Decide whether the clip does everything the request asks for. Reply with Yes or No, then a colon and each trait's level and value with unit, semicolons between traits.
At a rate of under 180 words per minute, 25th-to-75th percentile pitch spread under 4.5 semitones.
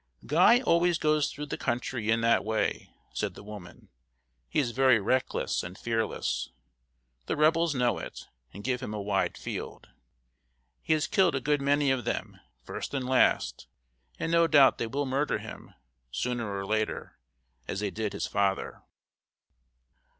No: average, 160 wpm; wide, 5.6 semitones